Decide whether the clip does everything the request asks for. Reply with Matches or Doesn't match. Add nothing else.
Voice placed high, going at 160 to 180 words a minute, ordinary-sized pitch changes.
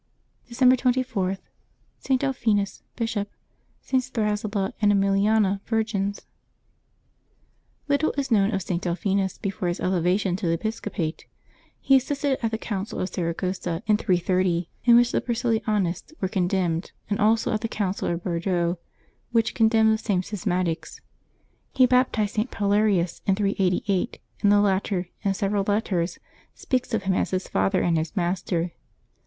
Doesn't match